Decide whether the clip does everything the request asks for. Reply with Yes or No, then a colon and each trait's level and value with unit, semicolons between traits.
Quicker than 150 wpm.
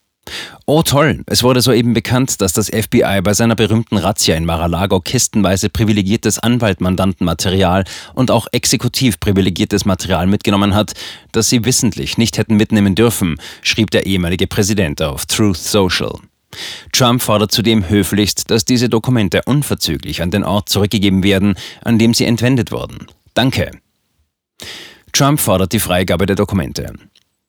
No: average, 140 wpm